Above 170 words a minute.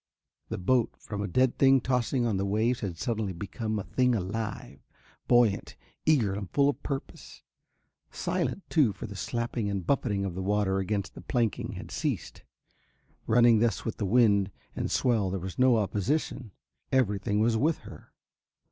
No: average, 165 wpm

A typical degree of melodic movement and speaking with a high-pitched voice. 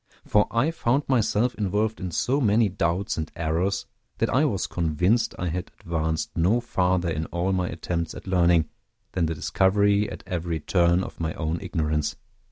No: average, 4.0 semitones; very low, 90 Hz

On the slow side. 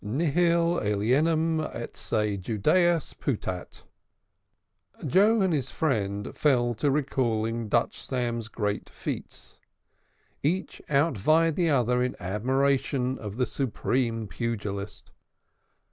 Yes: slow, 105 wpm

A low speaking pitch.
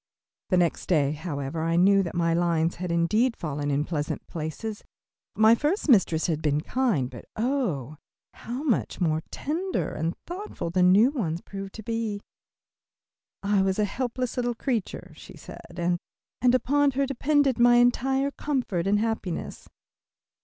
No: high, 200 Hz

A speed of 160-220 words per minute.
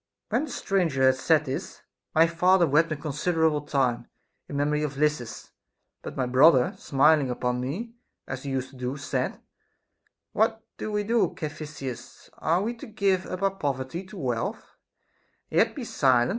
Yes: average, 175 wpm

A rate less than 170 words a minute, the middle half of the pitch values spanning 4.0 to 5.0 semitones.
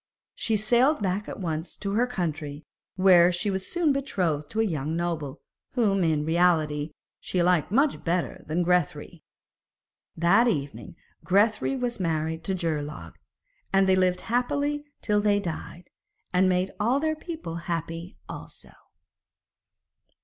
Yes: average, 140 wpm; average, 4.7 semitones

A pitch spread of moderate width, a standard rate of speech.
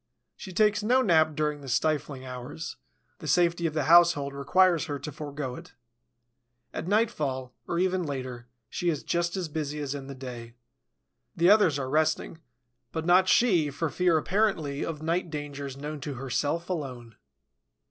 Yes: average, 3.7 semitones; average, 165 wpm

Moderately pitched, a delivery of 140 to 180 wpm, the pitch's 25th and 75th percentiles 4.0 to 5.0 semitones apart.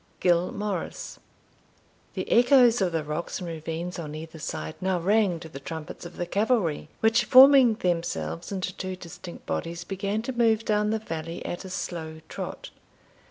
Yes: medium, 180 Hz; average, 165 wpm; average, 4.7 semitones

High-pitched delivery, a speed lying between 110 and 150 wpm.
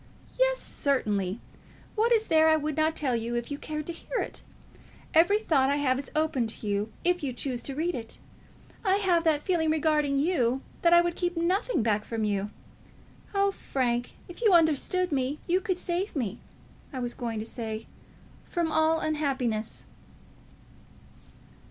No: very high, 305 Hz; average, 175 wpm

